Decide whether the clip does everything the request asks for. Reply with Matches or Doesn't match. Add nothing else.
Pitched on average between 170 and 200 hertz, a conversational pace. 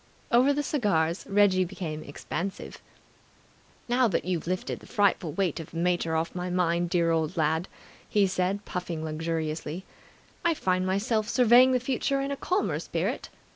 Matches